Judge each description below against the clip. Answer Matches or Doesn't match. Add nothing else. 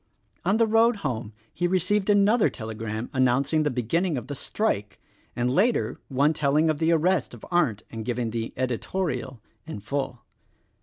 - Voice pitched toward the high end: Doesn't match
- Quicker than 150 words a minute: Matches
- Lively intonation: Matches